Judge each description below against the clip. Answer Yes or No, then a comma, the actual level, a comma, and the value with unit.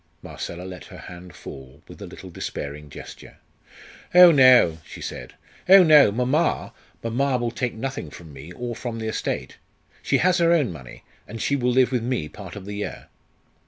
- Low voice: Yes, low, 115 Hz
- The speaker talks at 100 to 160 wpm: No, average, 185 wpm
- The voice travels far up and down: Yes, wide, 7.3 semitones